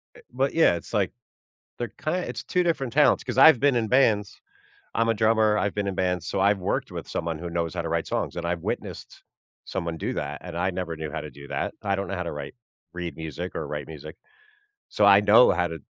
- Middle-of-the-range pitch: No, very low, 95 Hz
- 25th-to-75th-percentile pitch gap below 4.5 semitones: No, average, 5.1 semitones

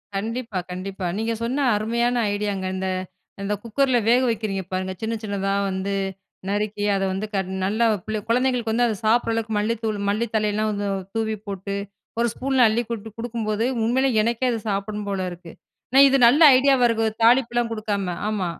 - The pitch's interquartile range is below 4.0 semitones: Yes, average, 2.8 semitones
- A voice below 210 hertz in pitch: No, high, 220 Hz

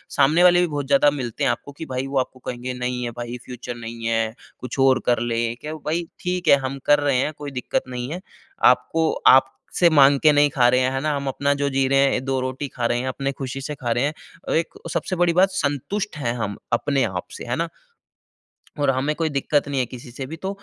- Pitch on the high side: No, low, 135 Hz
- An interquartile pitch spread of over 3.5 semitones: No, average, 2.8 semitones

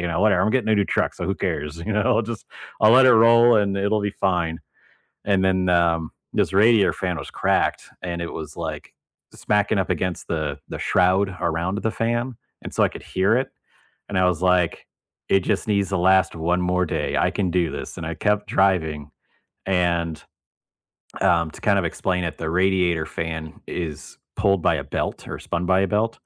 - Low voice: Yes, very low, 90 Hz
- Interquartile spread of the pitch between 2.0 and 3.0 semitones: No, average, 3.4 semitones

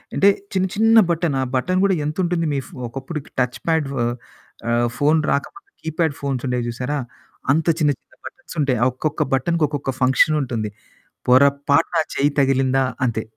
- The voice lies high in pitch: No, medium, 145 Hz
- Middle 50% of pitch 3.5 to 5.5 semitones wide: Yes, average, 3.9 semitones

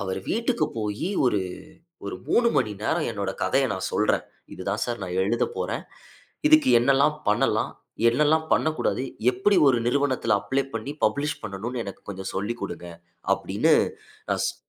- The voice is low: Yes, low, 120 Hz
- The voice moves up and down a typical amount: No, wide, 6.5 semitones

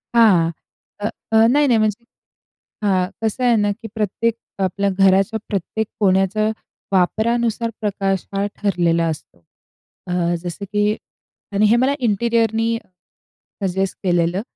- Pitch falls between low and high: No, high, 205 Hz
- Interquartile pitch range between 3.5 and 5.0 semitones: No, average, 2.9 semitones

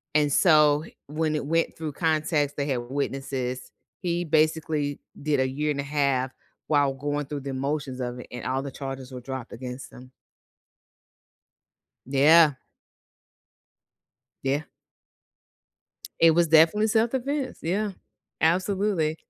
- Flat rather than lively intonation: No, average, 3.3 semitones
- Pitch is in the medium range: Yes, medium, 145 Hz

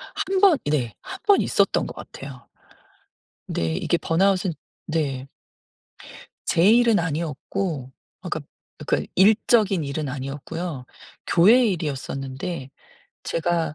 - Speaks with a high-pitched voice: No, medium, 165 Hz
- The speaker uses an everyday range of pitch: No, wide, 6.2 semitones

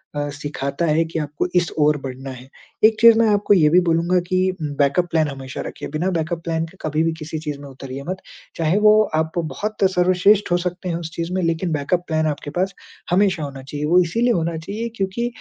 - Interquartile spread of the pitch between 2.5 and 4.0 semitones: Yes, average, 3.6 semitones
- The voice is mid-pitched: Yes, medium, 165 Hz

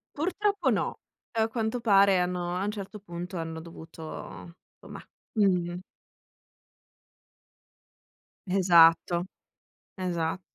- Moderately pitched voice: Yes, medium, 180 Hz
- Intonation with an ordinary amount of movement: Yes, average, 3.5 semitones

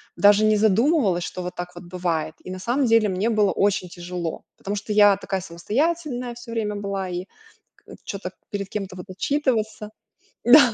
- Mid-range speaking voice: No, high, 205 Hz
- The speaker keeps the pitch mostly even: No, average, 3.8 semitones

